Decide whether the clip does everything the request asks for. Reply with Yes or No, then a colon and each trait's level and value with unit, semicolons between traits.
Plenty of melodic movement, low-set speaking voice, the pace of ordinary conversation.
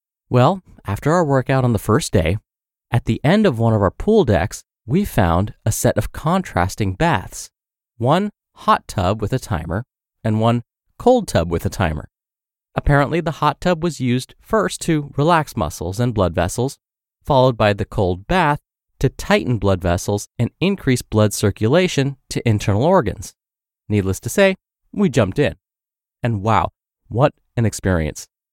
Yes: wide, 6.3 semitones; low, 120 Hz; average, 160 wpm